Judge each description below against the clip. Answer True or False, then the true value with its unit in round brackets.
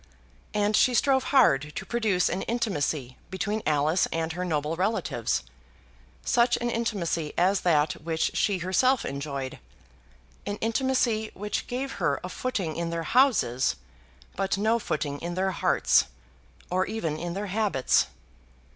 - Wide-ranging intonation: True (6.0 semitones)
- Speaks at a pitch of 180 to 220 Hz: True (185 Hz)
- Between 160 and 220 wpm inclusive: False (140 wpm)